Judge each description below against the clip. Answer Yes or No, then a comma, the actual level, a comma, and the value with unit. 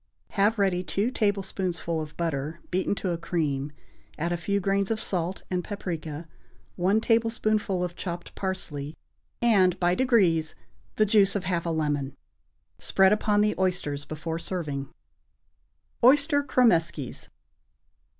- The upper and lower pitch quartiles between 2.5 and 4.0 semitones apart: Yes, average, 3.7 semitones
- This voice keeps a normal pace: No, slow, 130 wpm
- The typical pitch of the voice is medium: Yes, medium, 180 Hz